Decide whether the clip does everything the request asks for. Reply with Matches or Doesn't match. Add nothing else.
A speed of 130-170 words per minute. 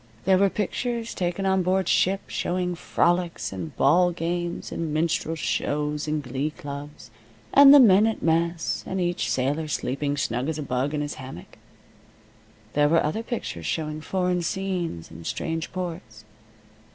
Matches